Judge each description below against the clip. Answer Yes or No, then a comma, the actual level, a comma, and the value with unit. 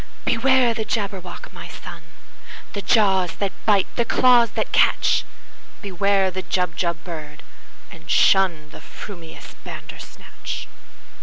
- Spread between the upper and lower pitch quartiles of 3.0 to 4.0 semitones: Yes, average, 3.5 semitones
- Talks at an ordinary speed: No, slow, 100 wpm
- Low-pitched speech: No, high, 195 Hz